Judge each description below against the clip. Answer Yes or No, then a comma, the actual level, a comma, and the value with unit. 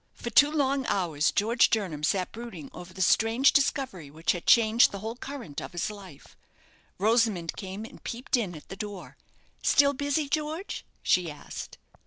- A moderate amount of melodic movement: No, wide, 6.3 semitones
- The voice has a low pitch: No, high, 215 Hz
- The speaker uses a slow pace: No, average, 170 wpm